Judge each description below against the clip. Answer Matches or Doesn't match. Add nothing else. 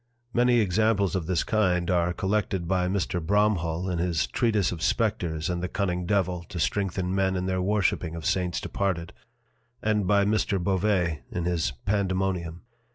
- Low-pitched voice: Matches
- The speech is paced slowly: Doesn't match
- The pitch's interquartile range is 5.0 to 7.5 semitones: Doesn't match